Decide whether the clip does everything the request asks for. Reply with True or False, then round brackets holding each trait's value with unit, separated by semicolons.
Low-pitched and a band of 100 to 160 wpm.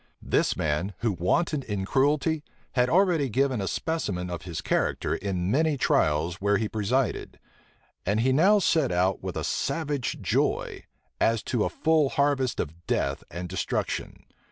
True (115 Hz; 155 wpm)